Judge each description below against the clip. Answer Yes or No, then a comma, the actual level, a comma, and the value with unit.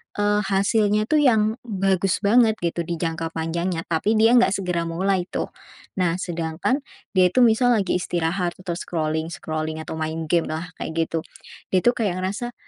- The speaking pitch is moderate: Yes, medium, 180 Hz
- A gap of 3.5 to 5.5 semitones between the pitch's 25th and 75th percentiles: Yes, average, 4.0 semitones